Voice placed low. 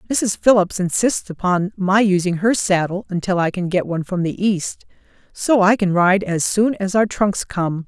No: high, 190 Hz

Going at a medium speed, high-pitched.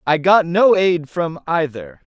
No: average, 170 wpm; medium, 170 Hz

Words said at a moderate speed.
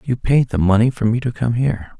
No: fast, 270 wpm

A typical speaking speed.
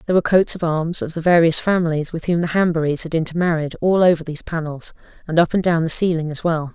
No: fast, 240 wpm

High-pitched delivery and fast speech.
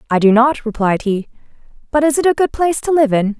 Yes: very high, 255 Hz; fast, 250 wpm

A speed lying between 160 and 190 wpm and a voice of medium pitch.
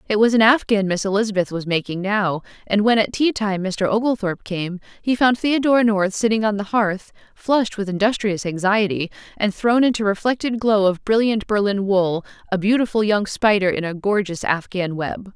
No: average, 185 wpm; high, 205 Hz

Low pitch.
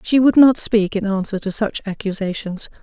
No: high, 210 Hz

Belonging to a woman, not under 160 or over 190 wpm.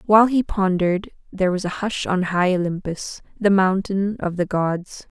Yes: female; average, 175 wpm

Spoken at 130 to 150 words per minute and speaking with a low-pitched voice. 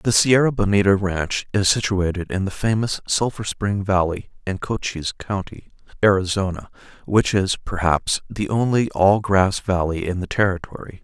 Yes: average, 145 wpm; very low, 95 Hz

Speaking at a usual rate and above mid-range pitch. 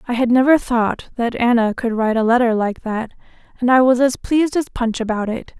No: fast, 225 wpm; high, 240 Hz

